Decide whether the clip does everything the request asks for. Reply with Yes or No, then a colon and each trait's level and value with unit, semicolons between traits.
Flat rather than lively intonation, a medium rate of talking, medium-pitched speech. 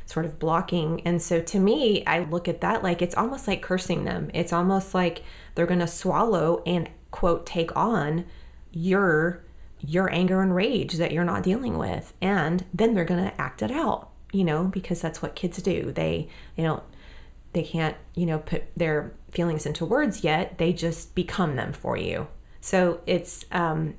Yes: narrow, 2.1 semitones; average, 190 wpm; medium, 170 Hz